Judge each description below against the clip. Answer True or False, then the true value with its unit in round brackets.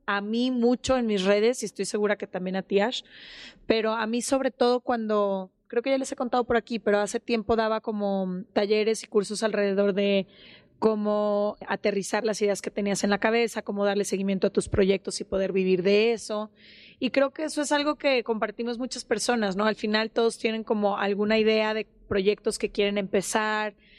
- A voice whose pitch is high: True (215 Hz)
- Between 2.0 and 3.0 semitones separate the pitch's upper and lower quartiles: True (2.4 semitones)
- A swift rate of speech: True (205 wpm)